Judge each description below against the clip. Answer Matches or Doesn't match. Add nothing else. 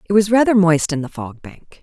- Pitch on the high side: Doesn't match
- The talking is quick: Matches